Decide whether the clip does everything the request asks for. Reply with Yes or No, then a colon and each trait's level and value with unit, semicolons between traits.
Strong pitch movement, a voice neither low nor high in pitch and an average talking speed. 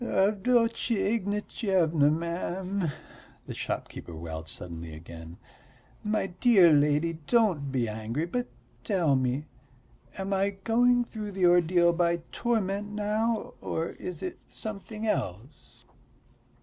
No: wide, 6.5 semitones; medium, 180 Hz; slow, 110 wpm